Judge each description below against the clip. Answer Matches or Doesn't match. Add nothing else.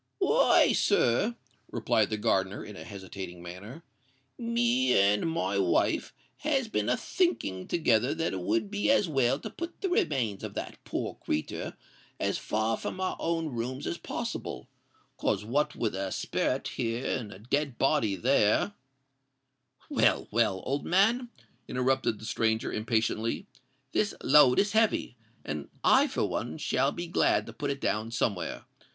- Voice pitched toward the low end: Matches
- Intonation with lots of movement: Matches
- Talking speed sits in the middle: Matches